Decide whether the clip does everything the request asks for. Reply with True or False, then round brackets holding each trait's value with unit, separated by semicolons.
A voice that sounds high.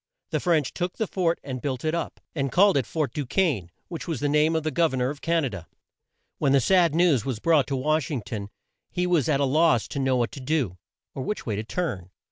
False (145 Hz)